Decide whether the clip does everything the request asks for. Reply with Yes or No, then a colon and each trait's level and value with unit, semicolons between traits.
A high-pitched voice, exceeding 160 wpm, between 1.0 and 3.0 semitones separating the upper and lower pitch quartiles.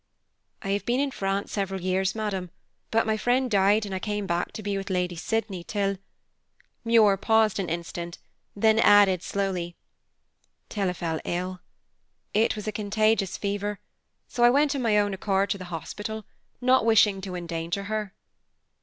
Yes: high, 200 Hz; average, 170 wpm; narrow, 2.6 semitones